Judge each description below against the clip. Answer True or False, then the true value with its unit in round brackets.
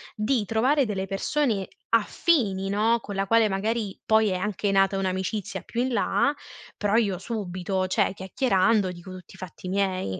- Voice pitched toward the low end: False (200 Hz)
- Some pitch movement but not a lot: True (3.1 semitones)